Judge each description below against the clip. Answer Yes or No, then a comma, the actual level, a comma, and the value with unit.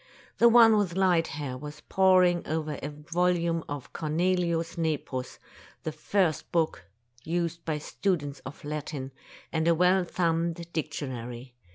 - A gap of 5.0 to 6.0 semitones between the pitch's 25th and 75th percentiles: No, average, 3.0 semitones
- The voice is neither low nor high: Yes, medium, 165 Hz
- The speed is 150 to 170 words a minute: No, slow, 135 wpm